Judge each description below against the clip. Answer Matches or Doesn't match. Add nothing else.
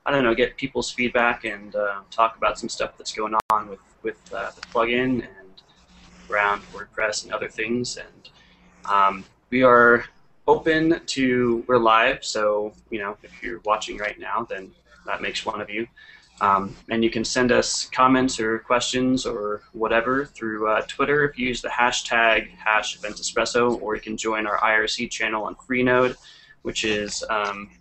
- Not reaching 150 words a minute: Doesn't match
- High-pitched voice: Doesn't match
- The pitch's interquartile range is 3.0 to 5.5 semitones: Doesn't match